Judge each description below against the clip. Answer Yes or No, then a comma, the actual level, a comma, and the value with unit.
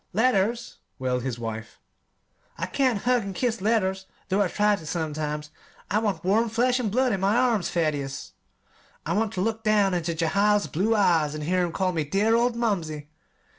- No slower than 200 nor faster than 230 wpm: No, average, 185 wpm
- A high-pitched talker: Yes, high, 195 Hz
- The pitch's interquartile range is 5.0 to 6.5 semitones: Yes, wide, 5.6 semitones